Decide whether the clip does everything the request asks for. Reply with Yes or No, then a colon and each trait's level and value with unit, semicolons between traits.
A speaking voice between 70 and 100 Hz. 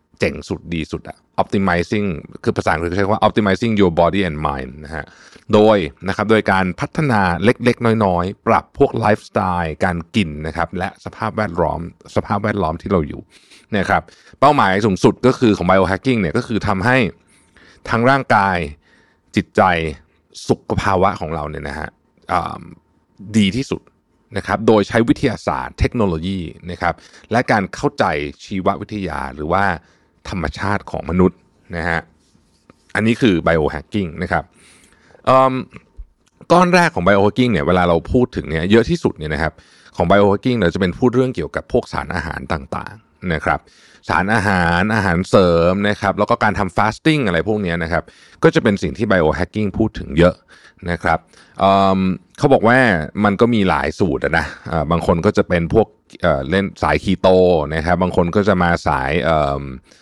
Yes: very low, 95 Hz